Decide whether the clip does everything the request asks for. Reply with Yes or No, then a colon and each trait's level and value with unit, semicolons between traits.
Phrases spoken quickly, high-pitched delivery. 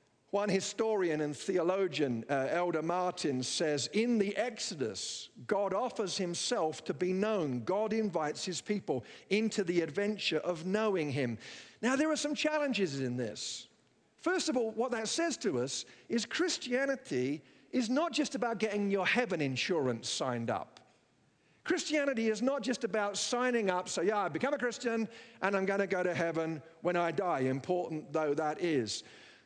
No: average, 165 wpm; high, 195 Hz